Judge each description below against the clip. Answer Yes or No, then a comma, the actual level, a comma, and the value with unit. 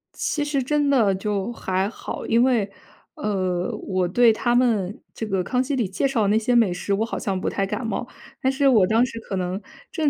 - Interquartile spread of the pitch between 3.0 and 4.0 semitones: No, average, 4.4 semitones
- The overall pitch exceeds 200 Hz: Yes, high, 220 Hz